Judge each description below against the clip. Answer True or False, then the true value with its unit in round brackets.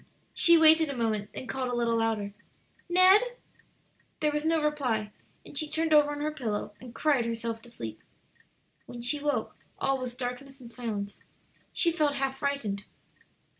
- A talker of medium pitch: False (265 Hz)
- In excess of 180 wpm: False (170 wpm)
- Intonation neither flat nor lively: True (4.6 semitones)